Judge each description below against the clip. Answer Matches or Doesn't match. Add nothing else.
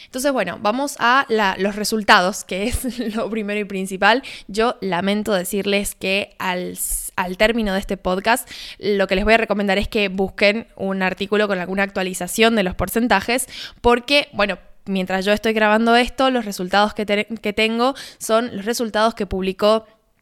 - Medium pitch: Doesn't match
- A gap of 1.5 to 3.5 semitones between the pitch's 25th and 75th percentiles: Matches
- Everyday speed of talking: Matches